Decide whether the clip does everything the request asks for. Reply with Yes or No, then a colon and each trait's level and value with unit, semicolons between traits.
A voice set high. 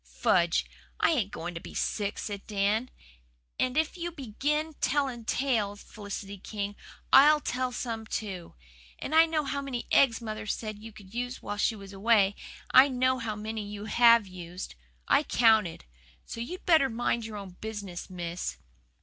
Yes: high, 220 Hz